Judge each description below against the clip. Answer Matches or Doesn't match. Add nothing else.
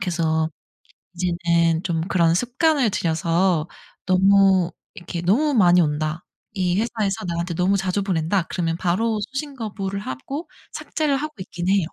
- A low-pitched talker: Doesn't match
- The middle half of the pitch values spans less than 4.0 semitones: Matches